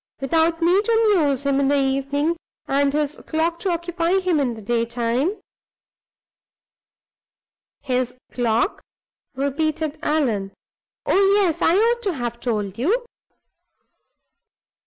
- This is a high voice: Yes, very high, 295 Hz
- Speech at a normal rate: No, slow, 120 wpm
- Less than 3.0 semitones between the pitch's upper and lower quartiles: No, average, 5.2 semitones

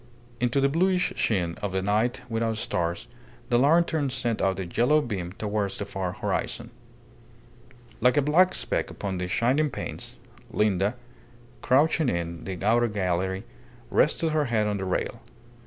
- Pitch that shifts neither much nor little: No, wide, 6.1 semitones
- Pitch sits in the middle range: No, low, 110 Hz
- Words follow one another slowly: No, average, 155 wpm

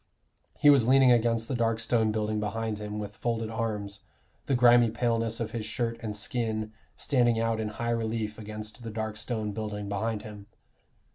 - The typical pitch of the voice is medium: No, low, 110 Hz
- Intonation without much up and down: Yes, narrow, 1.5 semitones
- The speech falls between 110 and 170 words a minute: No, average, 180 wpm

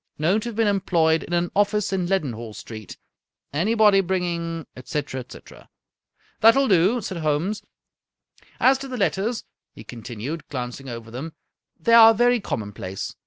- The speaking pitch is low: No, medium, 175 Hz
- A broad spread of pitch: Yes, wide, 7.6 semitones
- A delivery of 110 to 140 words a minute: No, average, 165 wpm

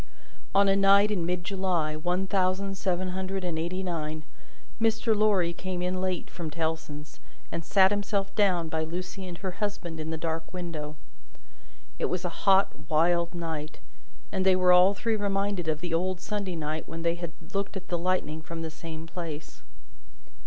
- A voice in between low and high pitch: Yes, medium, 180 Hz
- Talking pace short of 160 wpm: No, average, 180 wpm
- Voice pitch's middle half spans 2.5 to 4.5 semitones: Yes, average, 2.9 semitones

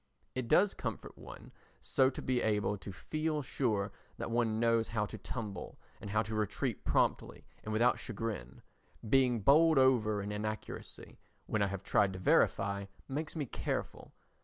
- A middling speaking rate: Yes, average, 160 wpm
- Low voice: Yes, low, 110 Hz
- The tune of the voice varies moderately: Yes, average, 4.0 semitones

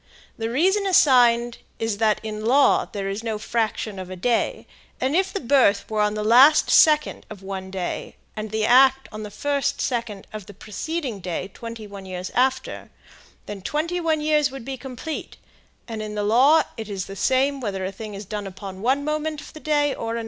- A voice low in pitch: No, high, 230 Hz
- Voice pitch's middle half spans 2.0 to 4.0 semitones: No, average, 5.2 semitones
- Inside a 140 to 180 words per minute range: No, fast, 205 wpm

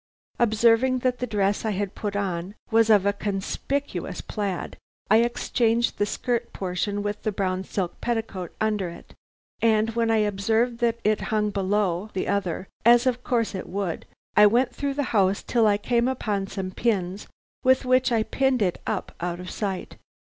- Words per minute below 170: No, average, 180 wpm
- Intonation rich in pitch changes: No, average, 3.3 semitones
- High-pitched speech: Yes, high, 210 Hz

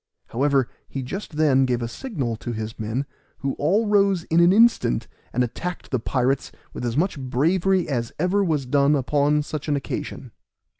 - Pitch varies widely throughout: Yes, wide, 5.7 semitones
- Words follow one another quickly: No, average, 180 wpm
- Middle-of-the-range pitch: Yes, medium, 145 Hz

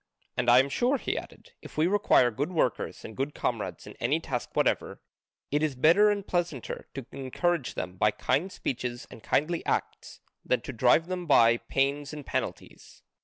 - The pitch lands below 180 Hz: Yes, medium, 140 Hz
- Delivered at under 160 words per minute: No, average, 180 wpm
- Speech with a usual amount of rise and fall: No, wide, 5.7 semitones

